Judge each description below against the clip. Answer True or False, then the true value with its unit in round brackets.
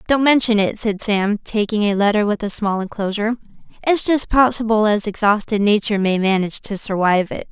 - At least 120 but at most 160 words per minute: False (185 wpm)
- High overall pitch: True (210 Hz)